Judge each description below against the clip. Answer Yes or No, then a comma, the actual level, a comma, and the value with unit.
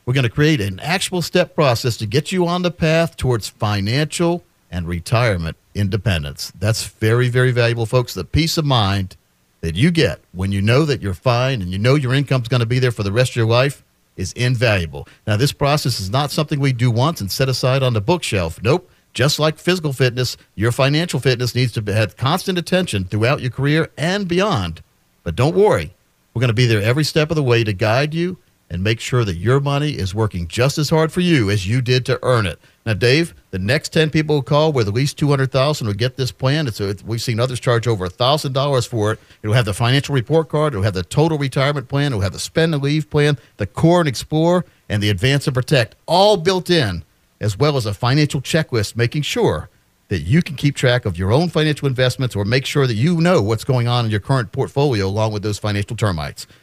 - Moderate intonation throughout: No, wide, 5.9 semitones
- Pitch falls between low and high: No, low, 125 Hz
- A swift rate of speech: Yes, fast, 230 wpm